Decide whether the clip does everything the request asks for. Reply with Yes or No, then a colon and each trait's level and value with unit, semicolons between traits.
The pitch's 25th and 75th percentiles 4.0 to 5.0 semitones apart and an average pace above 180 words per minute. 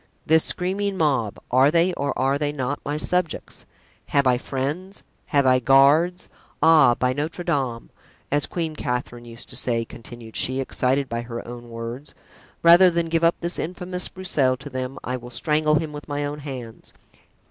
No: average, 4.4 semitones; average, 175 wpm